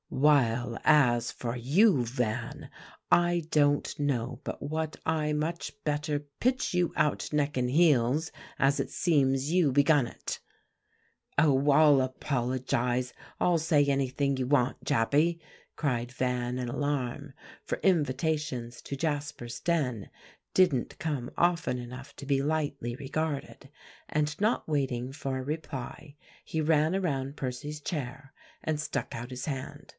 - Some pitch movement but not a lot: Yes, average, 3.4 semitones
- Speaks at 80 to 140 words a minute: Yes, slow, 135 wpm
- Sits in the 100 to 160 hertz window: Yes, medium, 140 Hz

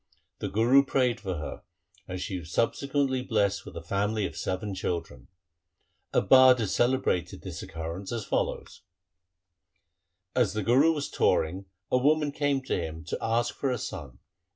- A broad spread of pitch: Yes, wide, 6.0 semitones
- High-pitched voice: No, low, 110 Hz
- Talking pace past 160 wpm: Yes, average, 170 wpm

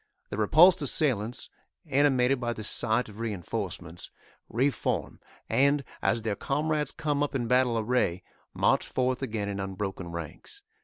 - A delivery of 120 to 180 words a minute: Yes, average, 140 wpm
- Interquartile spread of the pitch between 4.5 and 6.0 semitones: Yes, average, 5.2 semitones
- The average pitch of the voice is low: Yes, low, 120 Hz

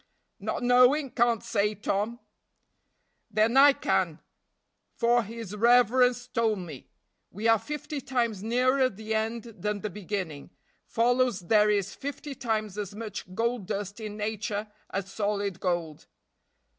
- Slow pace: Yes, slow, 130 wpm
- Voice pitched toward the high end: Yes, high, 220 Hz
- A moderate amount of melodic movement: Yes, average, 3.1 semitones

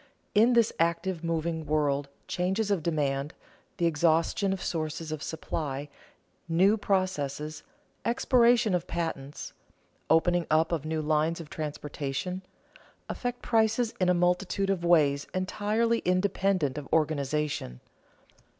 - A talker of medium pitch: Yes, medium, 165 Hz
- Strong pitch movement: No, average, 4.1 semitones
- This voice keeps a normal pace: No, slow, 120 wpm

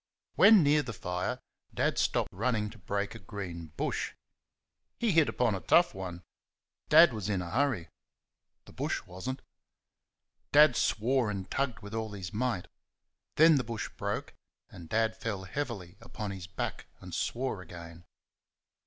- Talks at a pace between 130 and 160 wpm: Yes, average, 155 wpm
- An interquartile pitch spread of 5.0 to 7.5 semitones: Yes, wide, 5.5 semitones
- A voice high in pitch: No, low, 105 Hz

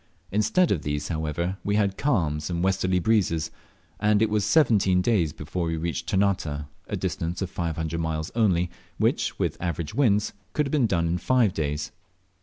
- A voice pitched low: Yes, very low, 90 Hz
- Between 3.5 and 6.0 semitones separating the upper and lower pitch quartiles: Yes, average, 4.4 semitones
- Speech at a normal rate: Yes, average, 180 wpm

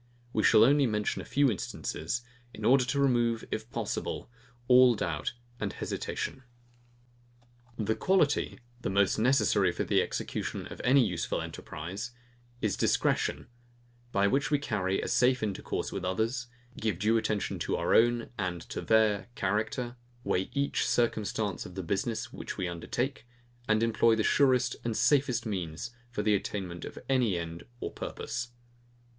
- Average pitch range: Yes, average, 4.0 semitones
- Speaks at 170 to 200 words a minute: No, average, 155 wpm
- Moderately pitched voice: No, low, 110 Hz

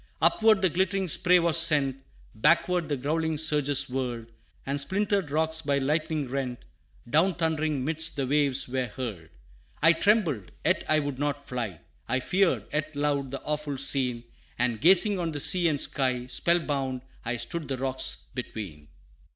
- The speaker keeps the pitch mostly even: No, average, 3.9 semitones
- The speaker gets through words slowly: No, average, 160 wpm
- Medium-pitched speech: Yes, medium, 145 Hz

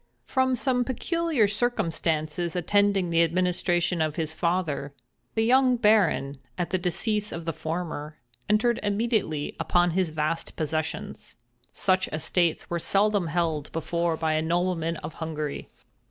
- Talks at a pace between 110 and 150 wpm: Yes, slow, 135 wpm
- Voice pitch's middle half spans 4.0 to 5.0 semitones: Yes, average, 4.5 semitones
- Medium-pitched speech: Yes, medium, 175 Hz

